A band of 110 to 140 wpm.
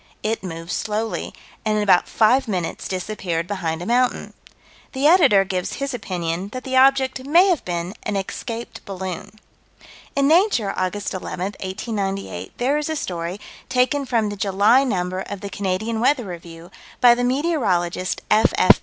No: average, 155 wpm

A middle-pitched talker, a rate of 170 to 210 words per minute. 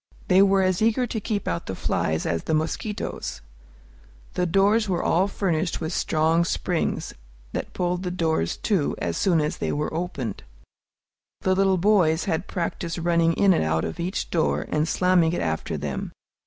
Yes: medium, 170 Hz; average, 175 wpm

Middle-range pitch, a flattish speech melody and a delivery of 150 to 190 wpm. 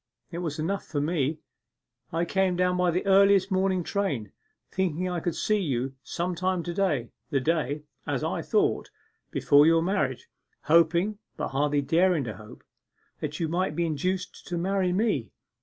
No: medium, 170 Hz; average, 4.0 semitones; average, 170 wpm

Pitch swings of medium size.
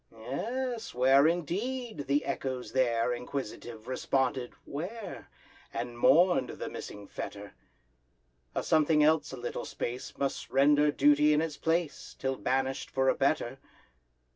Yes: average, 3.9 semitones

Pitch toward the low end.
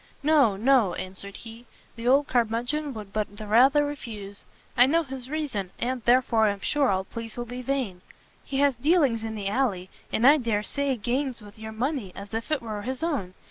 No: high, 235 Hz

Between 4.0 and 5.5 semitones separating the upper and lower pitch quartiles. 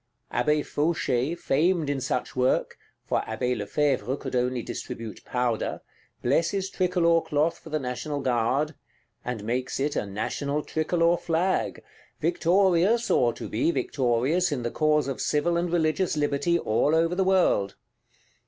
Yes: average, 5.2 semitones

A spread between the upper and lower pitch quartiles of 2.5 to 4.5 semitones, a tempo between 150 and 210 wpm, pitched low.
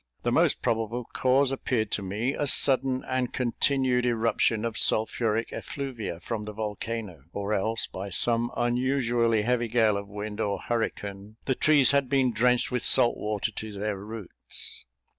Yes: average, 2.9 semitones; average, 160 wpm; low, 115 Hz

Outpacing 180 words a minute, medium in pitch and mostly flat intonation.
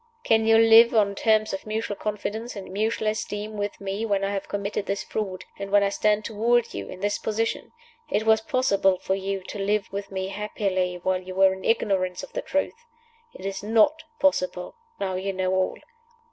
No: average, 200 wpm; high, 205 Hz; narrow, 2.3 semitones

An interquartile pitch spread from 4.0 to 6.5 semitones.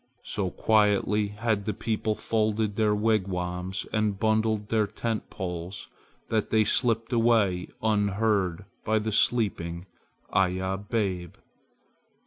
No: narrow, 2.5 semitones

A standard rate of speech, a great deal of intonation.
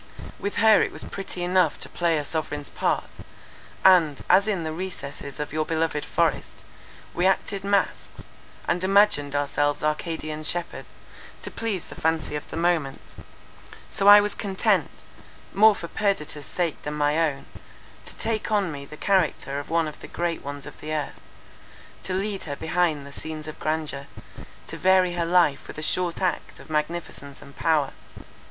No: average, 170 wpm; average, 4.0 semitones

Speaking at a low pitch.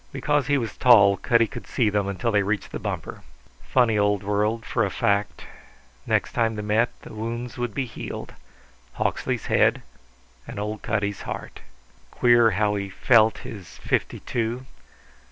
Yes: low, 110 Hz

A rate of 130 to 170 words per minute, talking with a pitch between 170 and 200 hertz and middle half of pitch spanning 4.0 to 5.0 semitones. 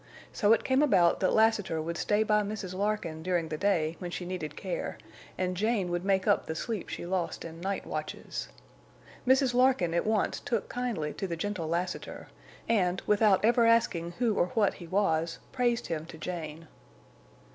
No: average, 180 wpm; high, 190 Hz; average, 4.3 semitones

